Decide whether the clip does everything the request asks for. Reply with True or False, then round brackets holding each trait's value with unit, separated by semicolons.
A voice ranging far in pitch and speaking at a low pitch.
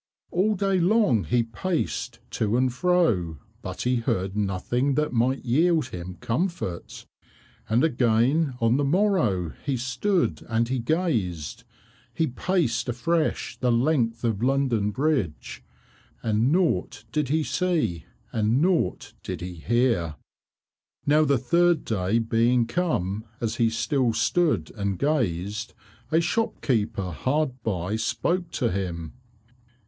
True (6.6 semitones; 120 Hz)